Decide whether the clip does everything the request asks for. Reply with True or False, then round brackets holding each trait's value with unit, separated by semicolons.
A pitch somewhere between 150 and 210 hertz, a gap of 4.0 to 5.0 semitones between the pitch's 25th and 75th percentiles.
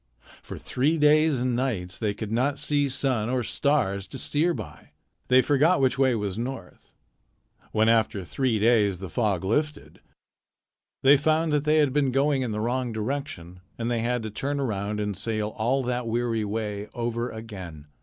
False (120 Hz; 4.4 semitones)